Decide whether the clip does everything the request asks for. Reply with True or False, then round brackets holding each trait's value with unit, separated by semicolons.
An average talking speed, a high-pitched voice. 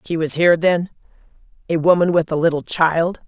False (165 wpm; 165 Hz)